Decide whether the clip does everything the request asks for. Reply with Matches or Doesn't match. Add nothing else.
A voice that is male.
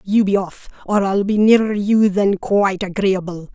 Doesn't match